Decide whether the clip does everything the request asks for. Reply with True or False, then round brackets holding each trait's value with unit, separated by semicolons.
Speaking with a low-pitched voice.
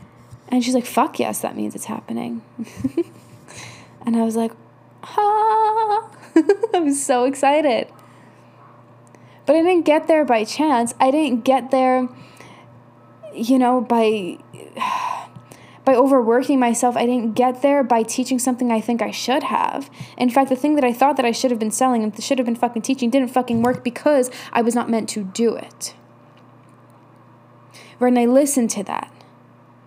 False (250 Hz)